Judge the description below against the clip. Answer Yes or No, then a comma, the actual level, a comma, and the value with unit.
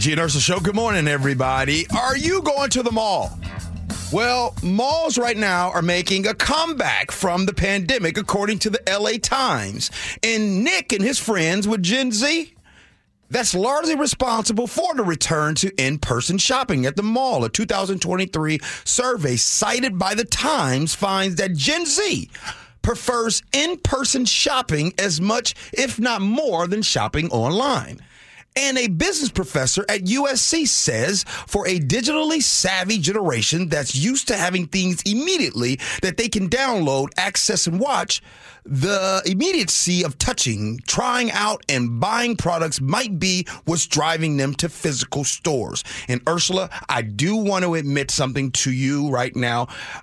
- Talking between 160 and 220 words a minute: No, average, 150 wpm